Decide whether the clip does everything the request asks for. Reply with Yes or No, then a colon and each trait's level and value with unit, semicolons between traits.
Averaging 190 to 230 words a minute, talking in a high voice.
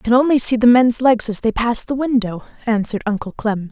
No: fast, 240 wpm; high, 235 Hz